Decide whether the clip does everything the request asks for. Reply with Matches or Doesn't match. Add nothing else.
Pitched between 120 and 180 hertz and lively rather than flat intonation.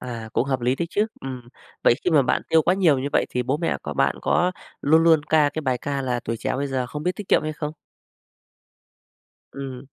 Doesn't match